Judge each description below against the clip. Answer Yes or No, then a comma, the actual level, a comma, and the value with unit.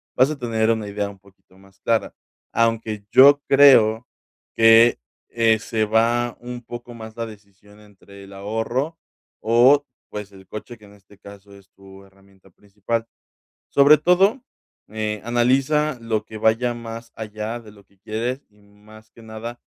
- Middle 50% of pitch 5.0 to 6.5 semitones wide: No, average, 2.7 semitones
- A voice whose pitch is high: No, low, 110 Hz